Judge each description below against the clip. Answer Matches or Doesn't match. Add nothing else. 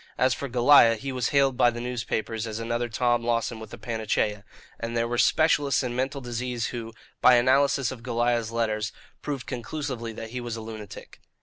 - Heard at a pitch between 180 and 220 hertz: Doesn't match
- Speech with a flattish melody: Matches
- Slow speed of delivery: Doesn't match